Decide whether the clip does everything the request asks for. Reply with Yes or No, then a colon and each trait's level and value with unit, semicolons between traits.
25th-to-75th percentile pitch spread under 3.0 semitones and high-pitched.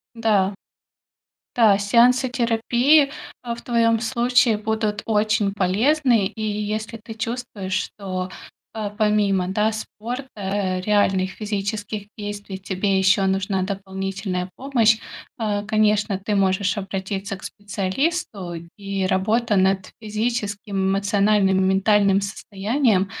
Yes: narrow, 2.6 semitones; high, 205 Hz